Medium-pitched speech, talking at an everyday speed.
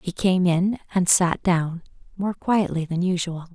Yes: medium, 180 Hz; average, 170 wpm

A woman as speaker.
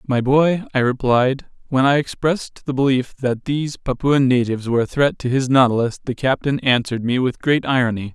No: male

